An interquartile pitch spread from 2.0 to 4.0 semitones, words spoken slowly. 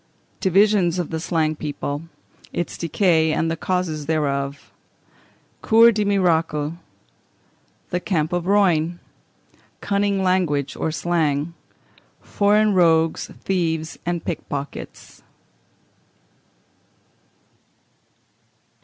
Yes: average, 3.3 semitones; slow, 85 wpm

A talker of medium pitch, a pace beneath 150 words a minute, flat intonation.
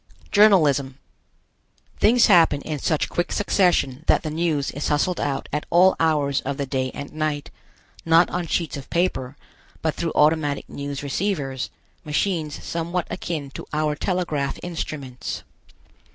No: medium, 155 Hz; average, 140 wpm; average, 3.4 semitones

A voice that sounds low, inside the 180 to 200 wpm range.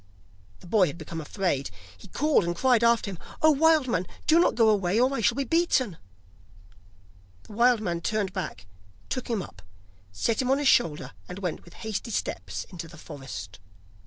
No: high, 205 Hz; average, 190 wpm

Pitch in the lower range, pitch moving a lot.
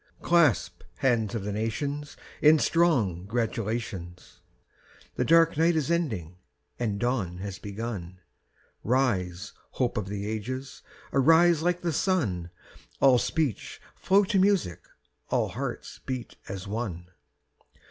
Yes: low, 120 Hz; wide, 7.8 semitones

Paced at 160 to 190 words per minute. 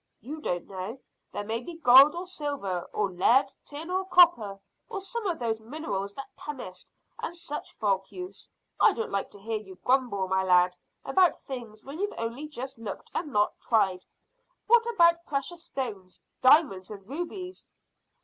Yes: average, 170 wpm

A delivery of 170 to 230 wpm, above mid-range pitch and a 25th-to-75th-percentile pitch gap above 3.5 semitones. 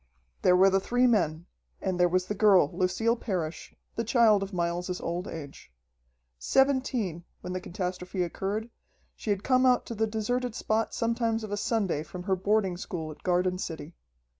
Yes: average, 175 wpm; high, 195 Hz; average, 3.9 semitones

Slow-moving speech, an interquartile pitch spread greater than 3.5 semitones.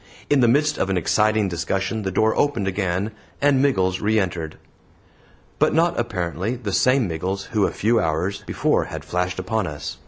No: average, 180 wpm; average, 4.2 semitones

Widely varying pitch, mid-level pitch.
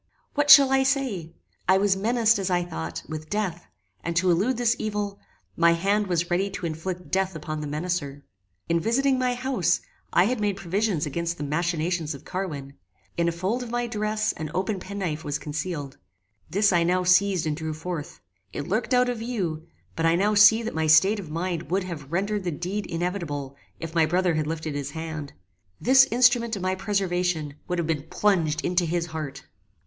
No: average, 4.5 semitones; medium, 180 Hz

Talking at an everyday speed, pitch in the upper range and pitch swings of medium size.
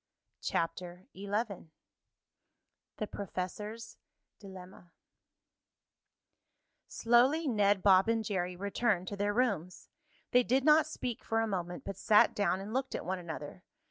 No: slow, 125 wpm; high, 200 Hz; average, 3.9 semitones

